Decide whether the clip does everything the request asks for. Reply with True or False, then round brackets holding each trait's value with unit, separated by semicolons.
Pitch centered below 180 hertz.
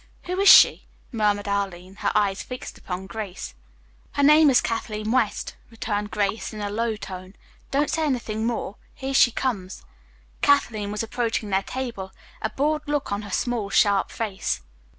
False (215 Hz)